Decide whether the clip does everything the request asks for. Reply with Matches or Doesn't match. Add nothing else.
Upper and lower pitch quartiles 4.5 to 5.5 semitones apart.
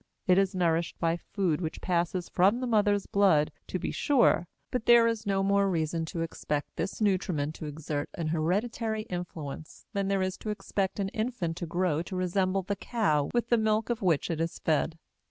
Doesn't match